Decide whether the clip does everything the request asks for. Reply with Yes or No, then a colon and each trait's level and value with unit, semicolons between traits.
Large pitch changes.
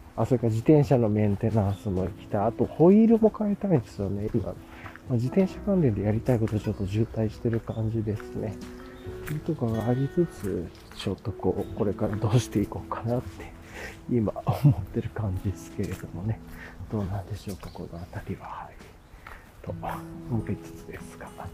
No: average, 4.0 semitones